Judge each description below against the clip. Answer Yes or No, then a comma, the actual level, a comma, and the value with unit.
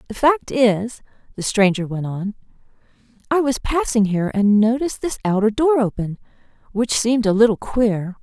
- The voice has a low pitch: No, high, 225 Hz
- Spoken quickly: No, average, 160 wpm